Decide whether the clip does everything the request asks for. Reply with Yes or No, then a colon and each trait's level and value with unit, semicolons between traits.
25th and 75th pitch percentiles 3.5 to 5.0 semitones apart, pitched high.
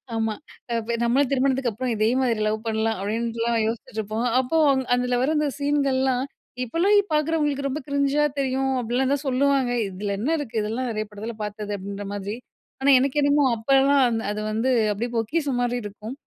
Yes: average, 3.9 semitones; high, 245 Hz